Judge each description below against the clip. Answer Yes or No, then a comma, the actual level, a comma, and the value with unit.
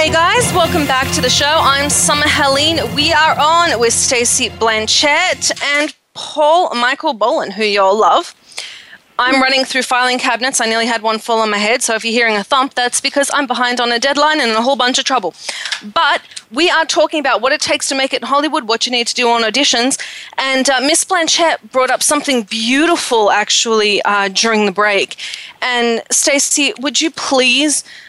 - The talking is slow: No, fast, 205 wpm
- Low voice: No, very high, 265 Hz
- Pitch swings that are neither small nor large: Yes, average, 4.4 semitones